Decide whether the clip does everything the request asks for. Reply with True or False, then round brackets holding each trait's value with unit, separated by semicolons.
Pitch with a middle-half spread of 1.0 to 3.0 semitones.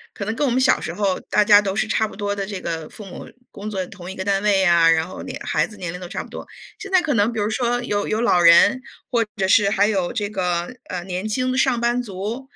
False (3.7 semitones)